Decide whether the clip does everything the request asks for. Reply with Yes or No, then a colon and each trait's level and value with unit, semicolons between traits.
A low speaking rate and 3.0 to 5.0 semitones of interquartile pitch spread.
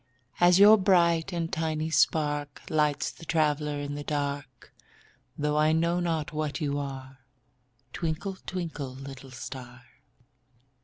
No: slow, 125 wpm; narrow, 2.6 semitones